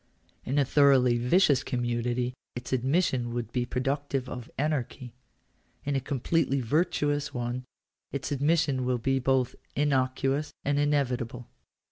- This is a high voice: No, low, 130 Hz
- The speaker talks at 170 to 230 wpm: No, average, 140 wpm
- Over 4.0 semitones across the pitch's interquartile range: No, narrow, 2.6 semitones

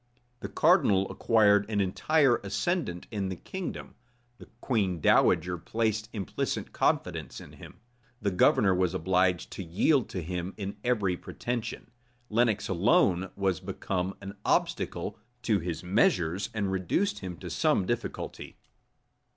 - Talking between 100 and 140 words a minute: Yes, slow, 135 wpm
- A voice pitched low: Yes, low, 100 Hz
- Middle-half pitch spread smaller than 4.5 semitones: Yes, average, 3.2 semitones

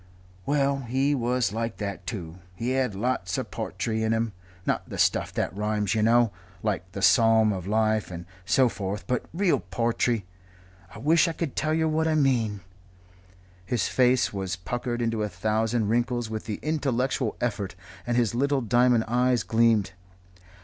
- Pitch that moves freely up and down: No, average, 3.4 semitones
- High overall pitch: No, low, 115 Hz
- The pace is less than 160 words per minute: No, average, 170 wpm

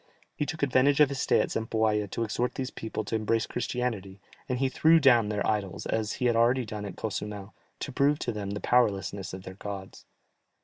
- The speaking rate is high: Yes, fast, 210 wpm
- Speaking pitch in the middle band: No, low, 110 Hz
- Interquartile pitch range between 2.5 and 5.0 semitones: Yes, average, 3.6 semitones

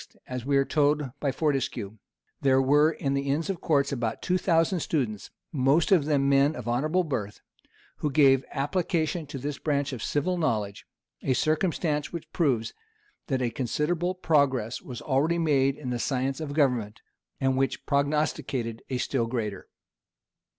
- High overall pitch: No, medium, 140 Hz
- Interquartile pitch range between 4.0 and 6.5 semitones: No, average, 3.2 semitones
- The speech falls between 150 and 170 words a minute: Yes, average, 160 wpm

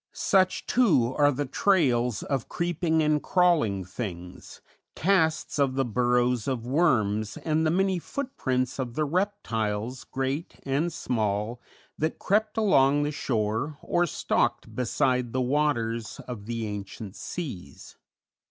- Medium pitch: No, low, 130 Hz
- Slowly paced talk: Yes, slow, 130 wpm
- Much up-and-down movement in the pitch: Yes, wide, 5.7 semitones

